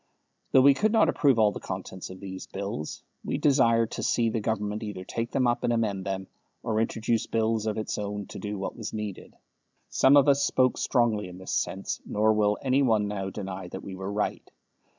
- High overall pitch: No, low, 110 Hz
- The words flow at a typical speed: No, fast, 210 wpm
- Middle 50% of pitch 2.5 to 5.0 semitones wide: Yes, average, 3.0 semitones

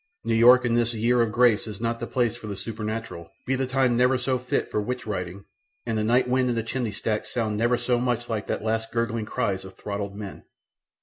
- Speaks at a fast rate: Yes, fast, 235 wpm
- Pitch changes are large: No, narrow, 2.4 semitones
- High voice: No, low, 115 Hz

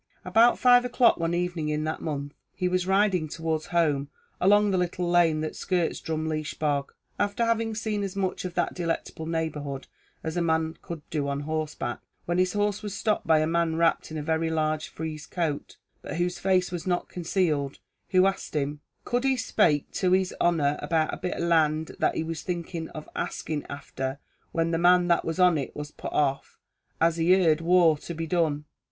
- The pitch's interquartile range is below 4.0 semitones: Yes, average, 2.8 semitones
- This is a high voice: No, medium, 165 Hz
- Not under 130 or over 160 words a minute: No, average, 200 wpm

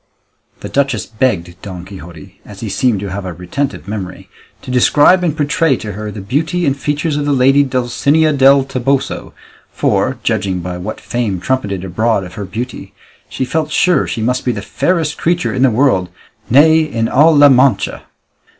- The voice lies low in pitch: Yes, low, 125 Hz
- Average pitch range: No, wide, 6.2 semitones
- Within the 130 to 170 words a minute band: No, average, 180 wpm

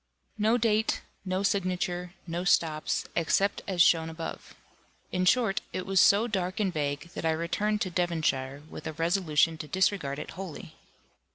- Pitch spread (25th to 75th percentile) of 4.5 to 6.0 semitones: No, average, 3.3 semitones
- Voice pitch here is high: No, medium, 180 Hz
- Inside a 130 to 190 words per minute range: Yes, average, 160 wpm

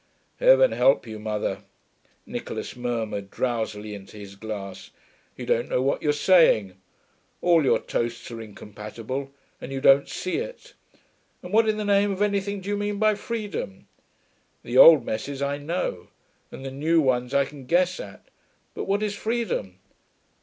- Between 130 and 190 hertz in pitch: Yes, medium, 140 Hz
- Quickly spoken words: No, average, 160 wpm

